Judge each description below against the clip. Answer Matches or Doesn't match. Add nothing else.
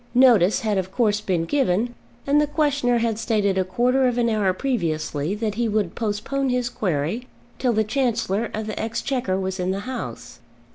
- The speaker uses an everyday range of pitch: Matches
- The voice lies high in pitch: Matches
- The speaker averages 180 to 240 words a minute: Matches